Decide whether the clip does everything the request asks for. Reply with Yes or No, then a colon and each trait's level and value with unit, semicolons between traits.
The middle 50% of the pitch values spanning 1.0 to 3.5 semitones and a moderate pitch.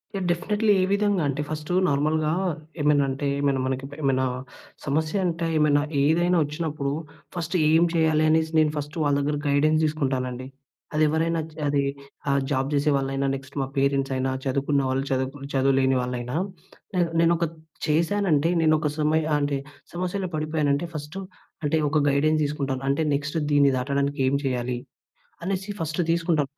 Yes: average, 2.7 semitones; medium, 150 Hz